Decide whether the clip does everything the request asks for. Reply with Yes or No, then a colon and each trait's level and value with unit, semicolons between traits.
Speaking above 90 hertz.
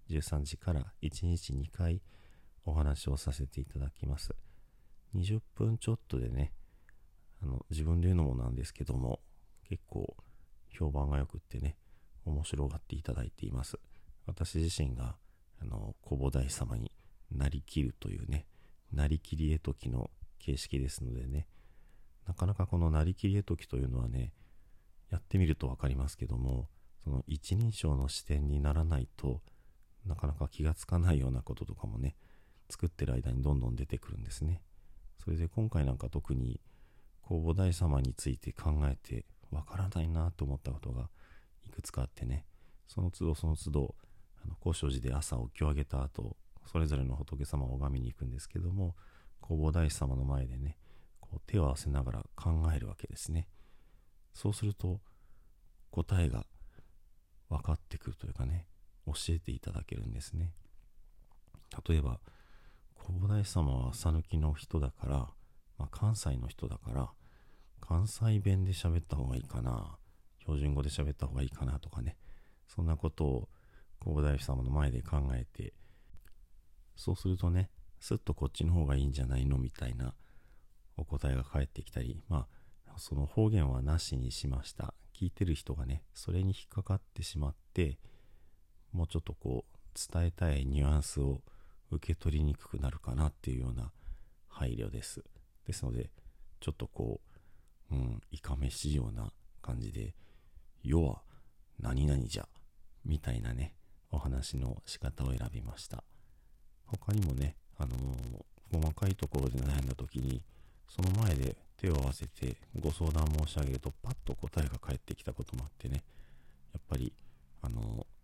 No: very low, 75 Hz